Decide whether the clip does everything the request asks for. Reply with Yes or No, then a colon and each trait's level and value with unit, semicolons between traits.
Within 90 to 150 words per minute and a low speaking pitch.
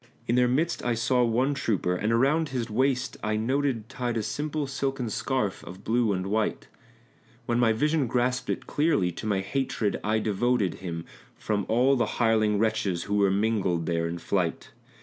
No: average, 180 wpm; low, 115 Hz